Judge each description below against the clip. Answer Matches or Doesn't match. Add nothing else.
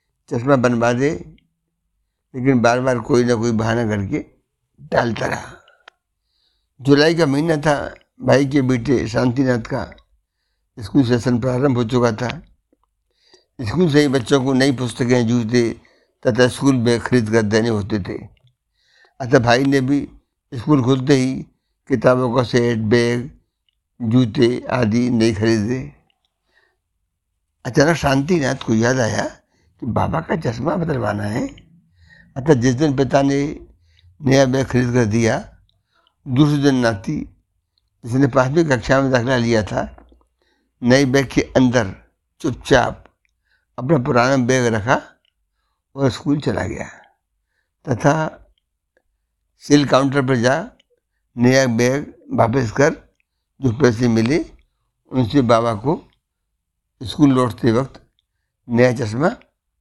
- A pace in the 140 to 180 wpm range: Doesn't match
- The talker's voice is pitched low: Matches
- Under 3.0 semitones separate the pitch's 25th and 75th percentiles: Doesn't match